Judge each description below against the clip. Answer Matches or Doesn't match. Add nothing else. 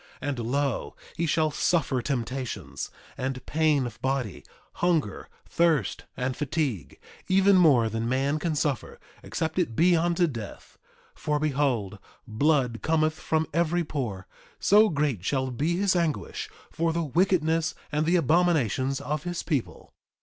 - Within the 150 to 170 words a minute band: Doesn't match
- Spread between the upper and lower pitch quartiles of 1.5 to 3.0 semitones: Doesn't match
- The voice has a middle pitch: Matches